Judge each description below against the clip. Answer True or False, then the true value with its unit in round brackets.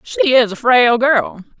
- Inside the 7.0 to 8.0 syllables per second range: False (5.1 syllables/s)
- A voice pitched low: False (235 Hz)